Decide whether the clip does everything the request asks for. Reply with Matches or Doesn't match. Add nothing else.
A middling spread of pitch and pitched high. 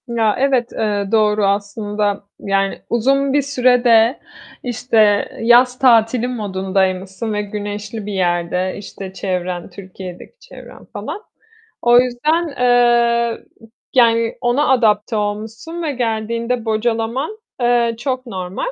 Matches